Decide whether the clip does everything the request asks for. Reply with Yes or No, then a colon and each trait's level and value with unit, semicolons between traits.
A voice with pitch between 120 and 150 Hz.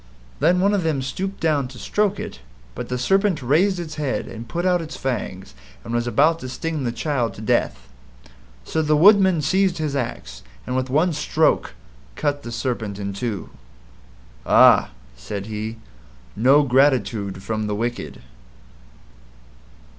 Yes: low, 135 Hz